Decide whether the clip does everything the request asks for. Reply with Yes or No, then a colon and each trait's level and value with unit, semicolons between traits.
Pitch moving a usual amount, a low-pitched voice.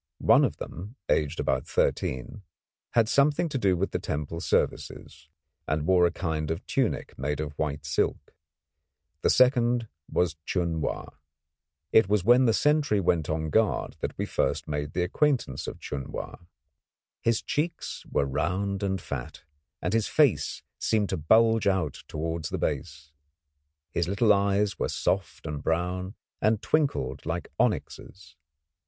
No: wide, 6.2 semitones; very low, 95 Hz